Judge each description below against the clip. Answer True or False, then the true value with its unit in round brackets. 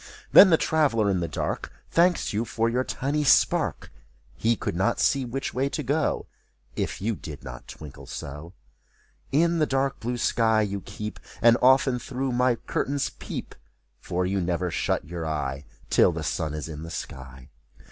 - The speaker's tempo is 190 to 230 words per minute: False (175 wpm)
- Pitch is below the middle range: True (115 Hz)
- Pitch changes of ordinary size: False (8.2 semitones)